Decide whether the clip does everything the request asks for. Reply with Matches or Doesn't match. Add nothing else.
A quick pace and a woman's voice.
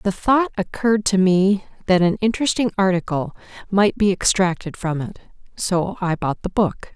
Doesn't match